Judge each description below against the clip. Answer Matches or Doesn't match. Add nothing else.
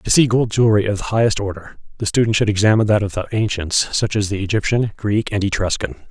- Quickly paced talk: Matches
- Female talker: Doesn't match